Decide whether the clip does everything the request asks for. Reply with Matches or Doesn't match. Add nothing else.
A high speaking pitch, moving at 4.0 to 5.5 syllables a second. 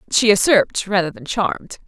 Doesn't match